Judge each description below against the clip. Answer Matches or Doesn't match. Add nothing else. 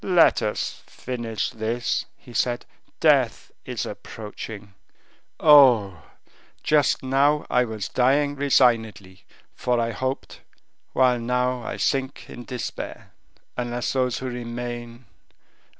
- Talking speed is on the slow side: Matches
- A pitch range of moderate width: Doesn't match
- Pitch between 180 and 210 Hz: Doesn't match